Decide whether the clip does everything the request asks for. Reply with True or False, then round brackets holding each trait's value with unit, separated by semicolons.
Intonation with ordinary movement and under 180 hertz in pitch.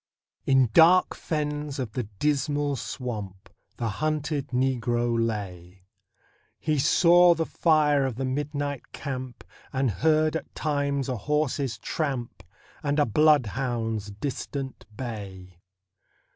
True (4.2 semitones; 135 Hz)